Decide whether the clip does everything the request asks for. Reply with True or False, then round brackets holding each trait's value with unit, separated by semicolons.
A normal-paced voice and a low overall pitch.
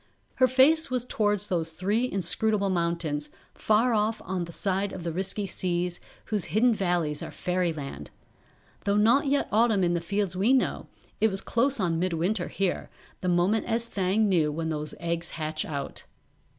False (175 wpm; 190 Hz)